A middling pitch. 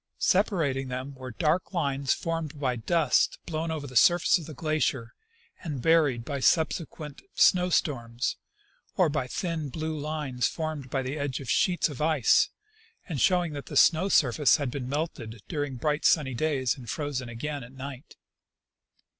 Yes: medium, 145 Hz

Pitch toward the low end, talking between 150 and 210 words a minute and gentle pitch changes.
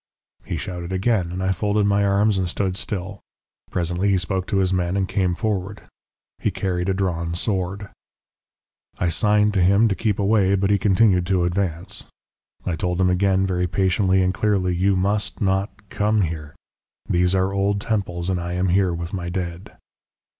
Yes: very low, 95 Hz; average, 180 wpm; narrow, 2.0 semitones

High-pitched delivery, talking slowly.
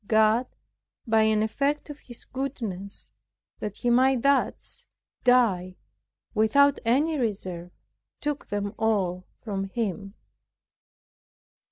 Yes: high, 220 Hz; slow, 100 wpm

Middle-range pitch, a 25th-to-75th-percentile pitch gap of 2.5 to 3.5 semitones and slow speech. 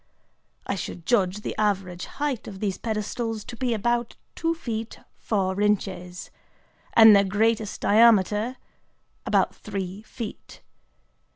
No: high, 210 Hz; average, 2.9 semitones; slow, 120 wpm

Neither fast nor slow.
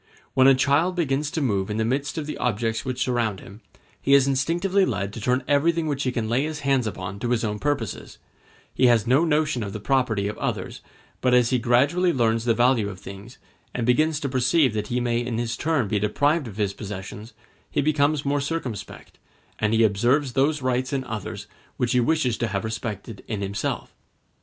No: fast, 210 wpm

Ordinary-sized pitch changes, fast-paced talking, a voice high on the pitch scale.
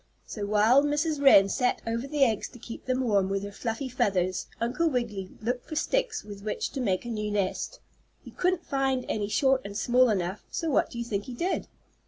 Yes: average, 4.8 semitones; fast, 215 wpm; high, 235 Hz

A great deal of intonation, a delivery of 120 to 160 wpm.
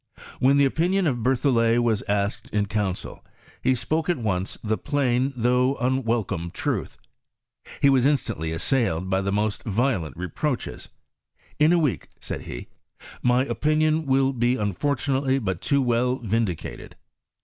No: average, 4.8 semitones; average, 150 wpm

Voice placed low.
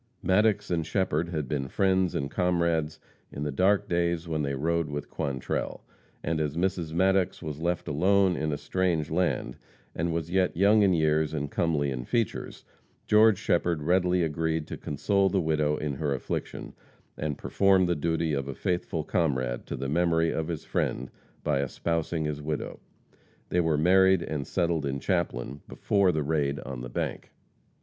Yes: very low, 80 Hz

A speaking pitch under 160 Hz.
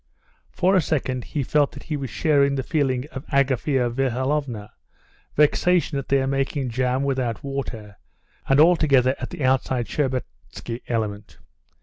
Yes: low, 135 Hz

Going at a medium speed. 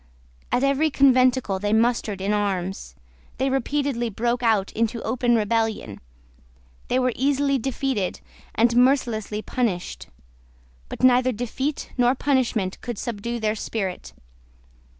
No: slow, 120 wpm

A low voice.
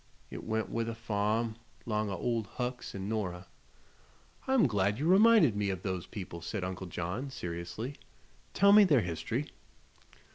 Yes: low, 110 Hz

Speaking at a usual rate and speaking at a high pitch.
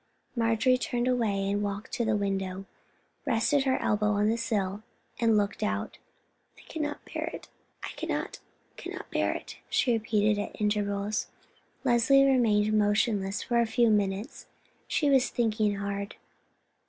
No: slow, 130 wpm; high, 215 Hz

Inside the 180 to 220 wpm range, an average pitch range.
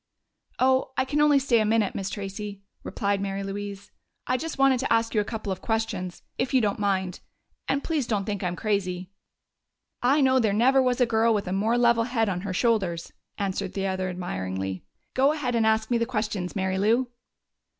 Yes: average, 200 wpm; average, 4.0 semitones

